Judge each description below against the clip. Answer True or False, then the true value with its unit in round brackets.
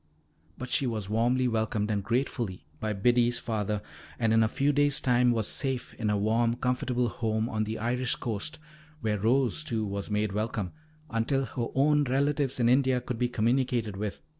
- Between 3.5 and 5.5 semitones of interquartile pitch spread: False (2.7 semitones)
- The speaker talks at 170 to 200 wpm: True (180 wpm)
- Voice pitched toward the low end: True (115 Hz)